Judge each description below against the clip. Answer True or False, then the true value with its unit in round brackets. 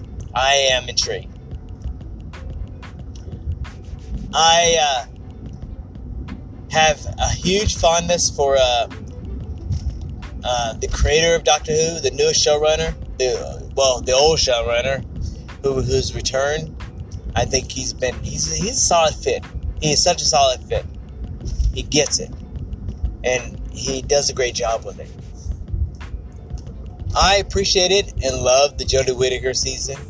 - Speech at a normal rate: False (125 wpm)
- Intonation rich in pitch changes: True (8.4 semitones)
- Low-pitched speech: True (105 Hz)